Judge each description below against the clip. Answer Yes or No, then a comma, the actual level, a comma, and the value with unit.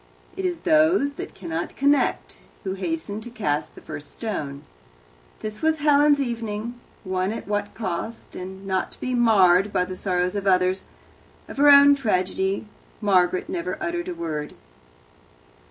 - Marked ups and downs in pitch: Yes, wide, 7.4 semitones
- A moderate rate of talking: Yes, average, 155 wpm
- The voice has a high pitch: Yes, high, 210 Hz